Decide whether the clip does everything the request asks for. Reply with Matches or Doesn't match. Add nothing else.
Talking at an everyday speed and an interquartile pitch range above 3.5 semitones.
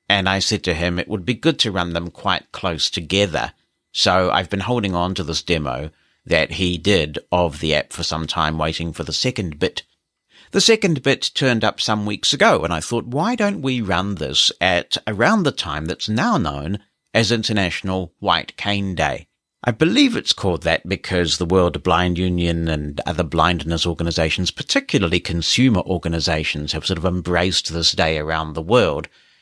Matches